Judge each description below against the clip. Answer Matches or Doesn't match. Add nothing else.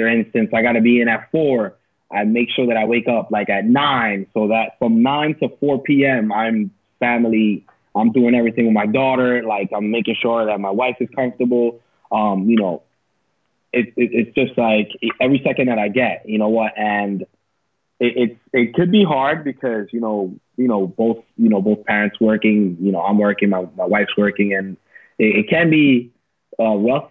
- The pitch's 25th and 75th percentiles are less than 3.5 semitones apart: Matches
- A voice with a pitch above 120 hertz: Doesn't match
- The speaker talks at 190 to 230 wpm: Matches